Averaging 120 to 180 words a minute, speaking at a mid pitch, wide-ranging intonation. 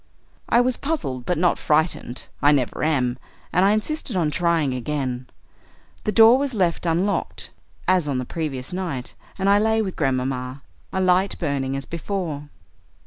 Yes: average, 160 wpm; medium, 165 Hz; wide, 6.3 semitones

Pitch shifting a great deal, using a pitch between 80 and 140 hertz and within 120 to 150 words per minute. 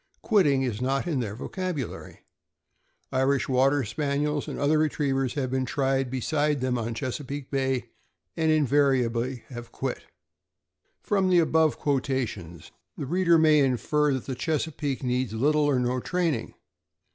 No: average, 2.9 semitones; low, 135 Hz; average, 145 wpm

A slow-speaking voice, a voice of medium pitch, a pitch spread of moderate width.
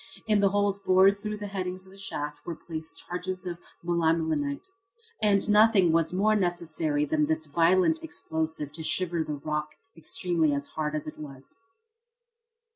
No: average, 155 wpm; medium, 170 Hz; average, 3.9 semitones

